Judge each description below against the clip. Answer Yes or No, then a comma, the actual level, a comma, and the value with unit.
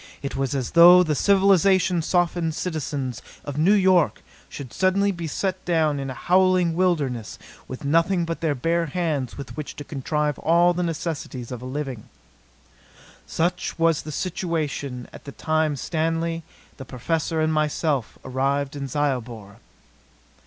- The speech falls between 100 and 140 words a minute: No, average, 150 wpm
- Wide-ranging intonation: No, average, 3.8 semitones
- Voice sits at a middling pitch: Yes, medium, 155 Hz